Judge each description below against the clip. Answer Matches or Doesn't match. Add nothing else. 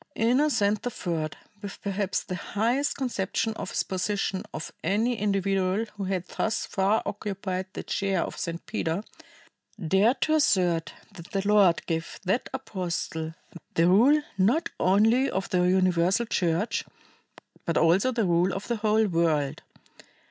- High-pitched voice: Matches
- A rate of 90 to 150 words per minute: Matches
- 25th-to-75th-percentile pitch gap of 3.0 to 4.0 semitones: Matches